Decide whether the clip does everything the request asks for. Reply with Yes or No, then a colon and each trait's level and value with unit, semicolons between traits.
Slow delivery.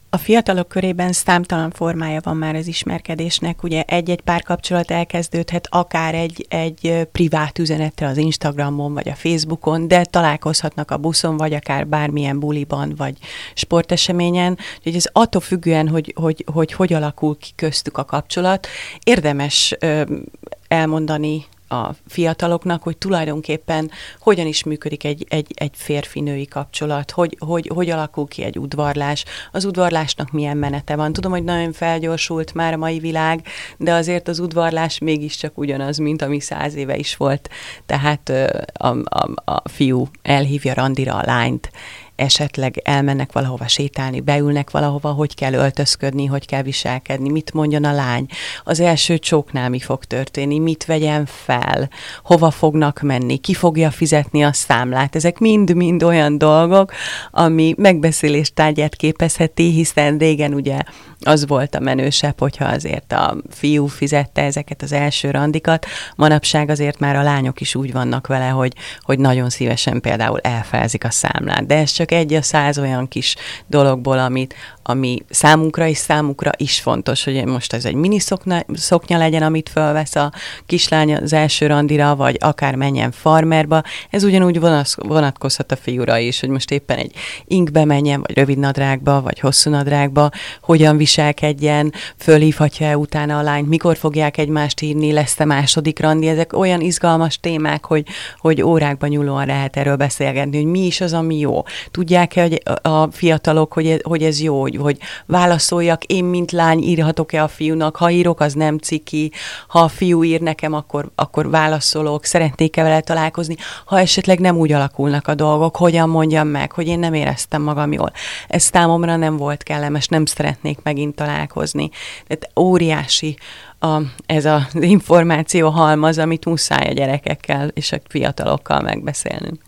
No: fast, 155 wpm